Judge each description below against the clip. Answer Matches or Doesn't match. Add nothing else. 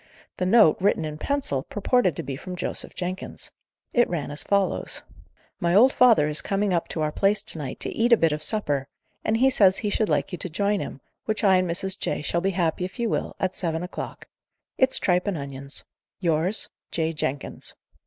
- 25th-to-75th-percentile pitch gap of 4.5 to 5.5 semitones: Matches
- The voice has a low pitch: Doesn't match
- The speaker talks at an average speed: Doesn't match